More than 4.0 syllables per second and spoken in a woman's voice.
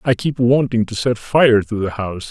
No: 5.0 syllables/s; male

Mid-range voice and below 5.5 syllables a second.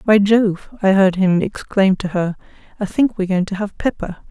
No: high, 195 Hz; 5.0 syllables/s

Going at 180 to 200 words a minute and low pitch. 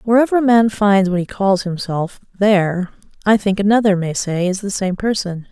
No: average, 195 wpm; high, 200 Hz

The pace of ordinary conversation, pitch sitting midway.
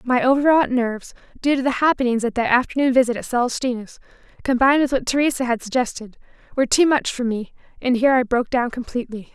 No: average, 195 wpm; very high, 250 Hz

